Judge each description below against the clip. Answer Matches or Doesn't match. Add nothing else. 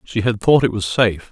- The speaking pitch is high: Doesn't match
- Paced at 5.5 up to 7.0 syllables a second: Matches